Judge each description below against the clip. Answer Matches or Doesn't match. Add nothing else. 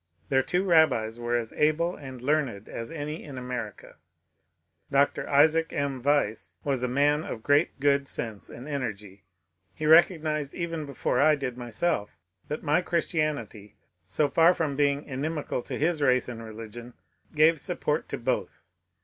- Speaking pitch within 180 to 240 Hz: Doesn't match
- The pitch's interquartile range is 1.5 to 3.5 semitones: Doesn't match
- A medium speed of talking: Matches